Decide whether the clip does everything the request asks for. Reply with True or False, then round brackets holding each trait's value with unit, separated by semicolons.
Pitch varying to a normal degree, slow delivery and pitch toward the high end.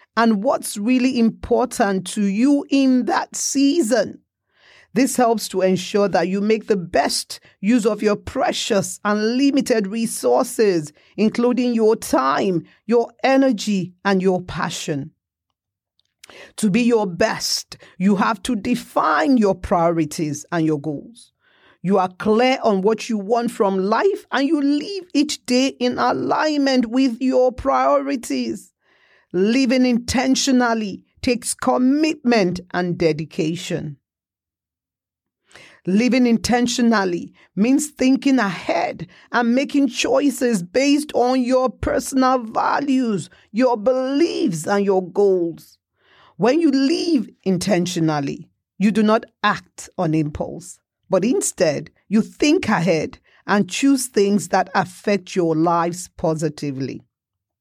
False (6.0 semitones; 115 wpm; 220 Hz)